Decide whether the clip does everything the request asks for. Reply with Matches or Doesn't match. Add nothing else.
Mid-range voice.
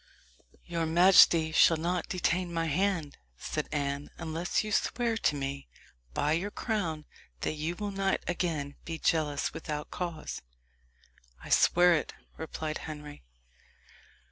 Matches